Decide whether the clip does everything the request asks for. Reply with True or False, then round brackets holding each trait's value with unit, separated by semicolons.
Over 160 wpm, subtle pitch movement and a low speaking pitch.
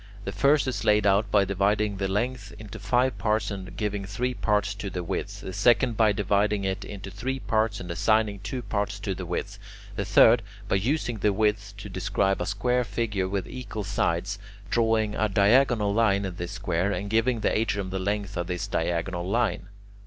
True (195 wpm; 2.2 semitones; 100 Hz)